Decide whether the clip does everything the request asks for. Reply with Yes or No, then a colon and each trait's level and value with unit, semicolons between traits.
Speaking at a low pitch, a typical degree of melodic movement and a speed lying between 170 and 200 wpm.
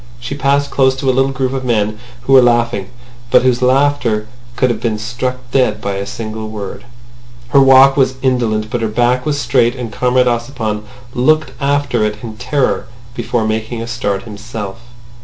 Yes: low, 120 Hz; average, 3.3 semitones; average, 180 wpm